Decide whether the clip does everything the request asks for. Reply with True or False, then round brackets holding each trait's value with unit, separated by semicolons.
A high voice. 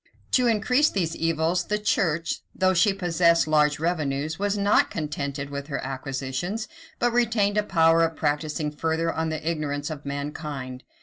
False (160 Hz)